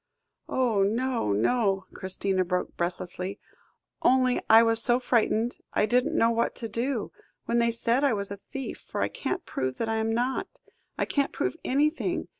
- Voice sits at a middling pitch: No, high, 230 Hz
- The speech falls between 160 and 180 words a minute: Yes, average, 175 wpm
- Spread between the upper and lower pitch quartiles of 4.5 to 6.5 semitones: No, average, 4.0 semitones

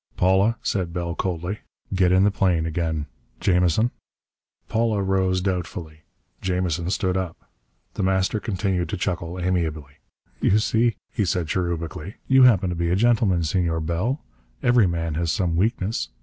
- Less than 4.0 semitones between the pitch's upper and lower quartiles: Yes, narrow, 2.6 semitones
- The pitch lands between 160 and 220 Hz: No, very low, 90 Hz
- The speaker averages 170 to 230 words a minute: No, average, 150 wpm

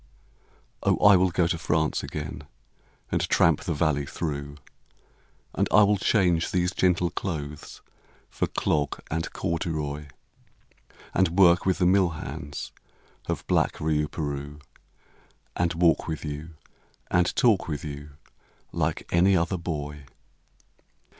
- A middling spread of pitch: Yes, average, 3.3 semitones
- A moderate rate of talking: No, slow, 125 wpm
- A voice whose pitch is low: Yes, very low, 85 Hz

